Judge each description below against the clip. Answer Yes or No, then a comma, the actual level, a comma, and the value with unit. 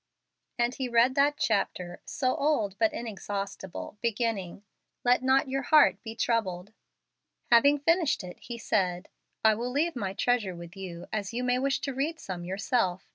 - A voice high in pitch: Yes, high, 230 Hz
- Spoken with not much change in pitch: No, average, 5.3 semitones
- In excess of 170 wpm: No, average, 165 wpm